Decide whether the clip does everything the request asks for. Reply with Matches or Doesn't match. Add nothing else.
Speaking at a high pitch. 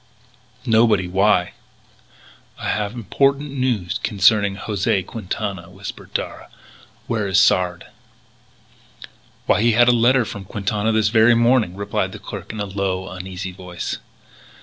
Doesn't match